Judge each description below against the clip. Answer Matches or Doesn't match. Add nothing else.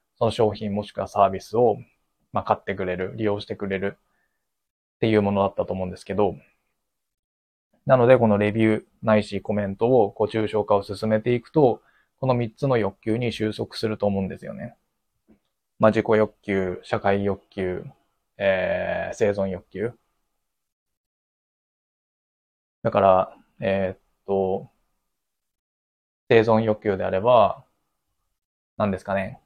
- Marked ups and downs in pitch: Doesn't match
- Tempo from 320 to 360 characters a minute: Doesn't match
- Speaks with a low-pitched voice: Matches